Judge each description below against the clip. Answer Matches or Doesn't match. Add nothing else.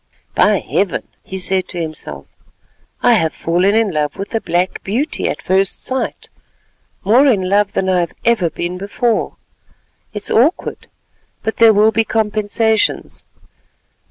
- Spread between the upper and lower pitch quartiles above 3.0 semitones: Matches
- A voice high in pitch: Matches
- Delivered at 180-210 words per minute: Doesn't match